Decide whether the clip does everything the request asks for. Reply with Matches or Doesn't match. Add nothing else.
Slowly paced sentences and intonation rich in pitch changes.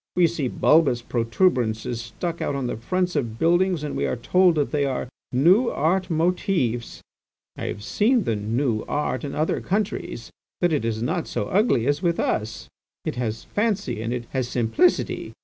Doesn't match